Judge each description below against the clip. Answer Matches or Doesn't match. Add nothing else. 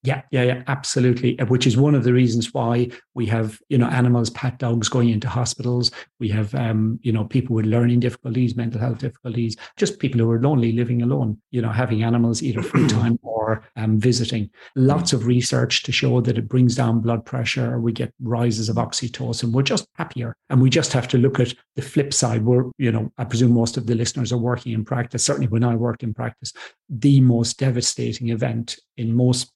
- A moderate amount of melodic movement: Doesn't match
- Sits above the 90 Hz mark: Matches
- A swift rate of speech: Matches